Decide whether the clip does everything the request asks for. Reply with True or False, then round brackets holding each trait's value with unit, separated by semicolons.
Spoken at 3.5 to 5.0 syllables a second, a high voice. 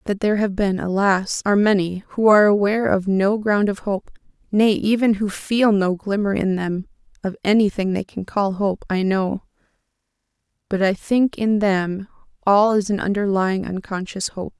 True (4.7 syllables/s; 200 Hz)